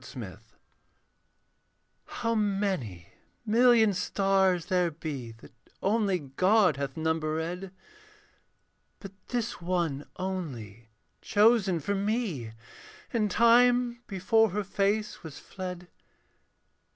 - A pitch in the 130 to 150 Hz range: No, high, 190 Hz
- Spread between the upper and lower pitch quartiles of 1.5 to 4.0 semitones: No, average, 5.1 semitones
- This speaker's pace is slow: Yes, slow, 95 wpm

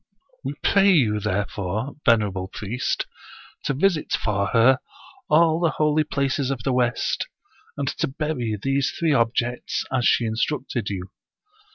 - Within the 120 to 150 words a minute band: Yes, average, 140 wpm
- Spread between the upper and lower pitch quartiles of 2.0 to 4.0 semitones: No, average, 5.3 semitones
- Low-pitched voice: Yes, low, 125 Hz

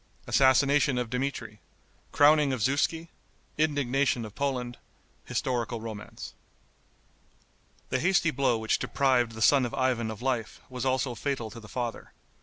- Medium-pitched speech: No, low, 130 Hz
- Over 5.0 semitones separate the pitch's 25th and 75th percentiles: No, average, 3.1 semitones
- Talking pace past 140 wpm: No, slow, 135 wpm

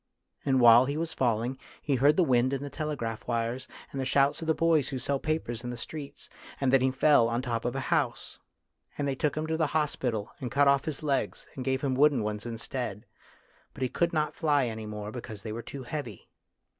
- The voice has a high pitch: No, low, 130 Hz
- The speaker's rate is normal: No, fast, 230 wpm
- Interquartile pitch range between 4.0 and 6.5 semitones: No, average, 3.5 semitones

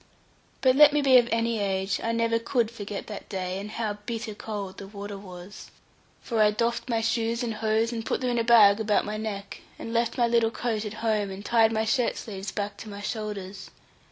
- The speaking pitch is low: No, high, 220 Hz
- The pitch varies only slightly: Yes, narrow, 2.3 semitones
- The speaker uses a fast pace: Yes, fast, 220 wpm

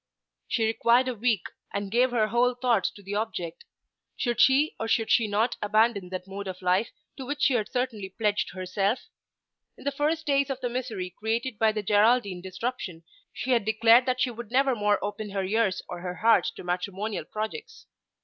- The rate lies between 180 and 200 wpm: Yes, average, 195 wpm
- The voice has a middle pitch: No, high, 220 Hz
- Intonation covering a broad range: No, average, 3.7 semitones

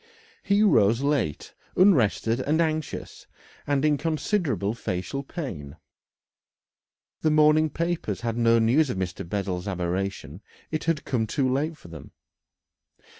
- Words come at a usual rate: No, slow, 125 wpm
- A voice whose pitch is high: No, low, 130 Hz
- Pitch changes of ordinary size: No, wide, 7.8 semitones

